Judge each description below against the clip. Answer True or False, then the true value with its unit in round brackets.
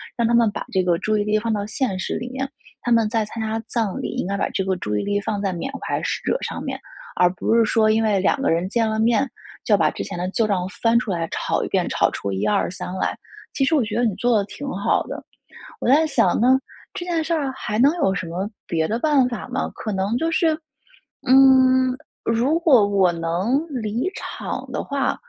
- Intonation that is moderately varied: True (5.0 semitones)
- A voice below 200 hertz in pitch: False (225 Hz)